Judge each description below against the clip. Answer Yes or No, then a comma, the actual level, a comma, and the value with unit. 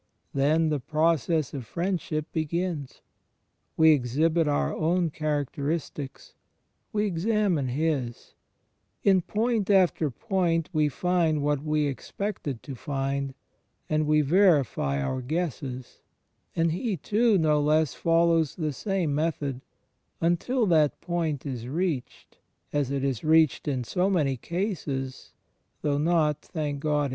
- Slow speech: Yes, slow, 125 wpm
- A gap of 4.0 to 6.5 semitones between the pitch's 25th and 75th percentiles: No, average, 3.5 semitones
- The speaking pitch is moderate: Yes, medium, 155 Hz